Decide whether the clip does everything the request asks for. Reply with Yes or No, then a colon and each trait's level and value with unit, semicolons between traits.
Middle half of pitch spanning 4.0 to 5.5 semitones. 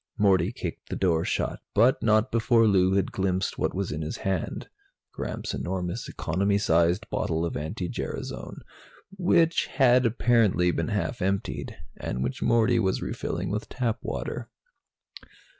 Yes: average, 4.7 semitones